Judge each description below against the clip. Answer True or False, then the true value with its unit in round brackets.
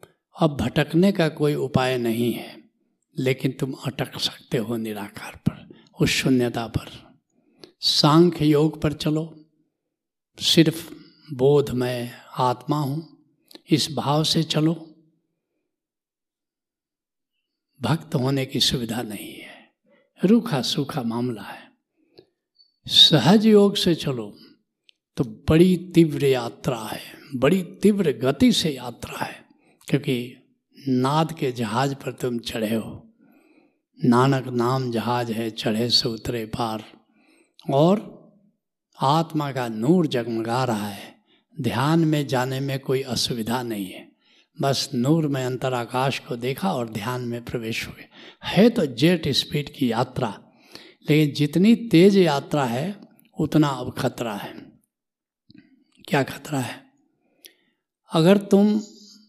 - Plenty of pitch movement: True (5.8 semitones)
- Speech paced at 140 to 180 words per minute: False (120 wpm)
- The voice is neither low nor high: True (145 Hz)